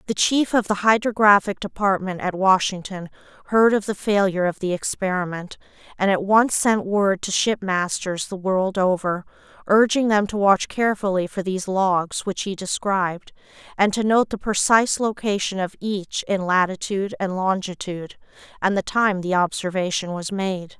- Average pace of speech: Yes, average, 160 wpm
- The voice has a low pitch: No, high, 195 Hz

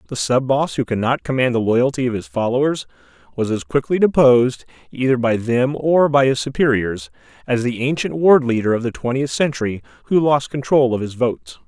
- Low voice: Yes, low, 130 Hz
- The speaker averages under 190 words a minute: No, average, 195 wpm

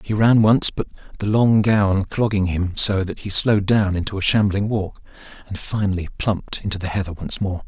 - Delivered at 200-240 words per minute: Yes, fast, 205 wpm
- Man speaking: Yes, male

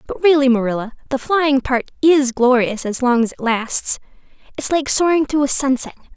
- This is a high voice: Yes, very high, 265 Hz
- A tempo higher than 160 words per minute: Yes, average, 185 wpm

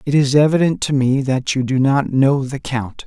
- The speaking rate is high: Yes, fast, 235 wpm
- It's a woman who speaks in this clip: No, male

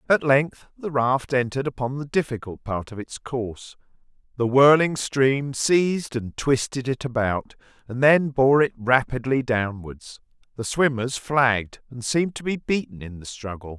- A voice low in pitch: Yes, low, 130 Hz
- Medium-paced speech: Yes, average, 160 wpm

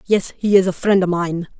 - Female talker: Yes, female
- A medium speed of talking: No, fast, 265 wpm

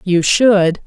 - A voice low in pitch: No, high, 190 Hz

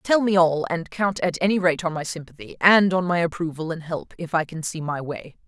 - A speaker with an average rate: No, fast, 250 wpm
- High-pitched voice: No, medium, 170 Hz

